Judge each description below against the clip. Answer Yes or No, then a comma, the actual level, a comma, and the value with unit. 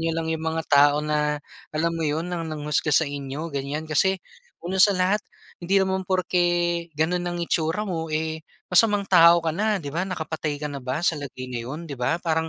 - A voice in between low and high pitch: Yes, medium, 160 Hz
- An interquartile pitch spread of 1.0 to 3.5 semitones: Yes, average, 2.8 semitones